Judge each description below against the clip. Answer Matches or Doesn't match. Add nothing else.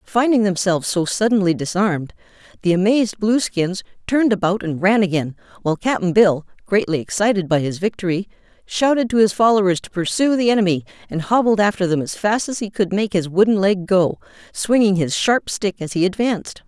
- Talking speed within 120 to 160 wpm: Doesn't match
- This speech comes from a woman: Matches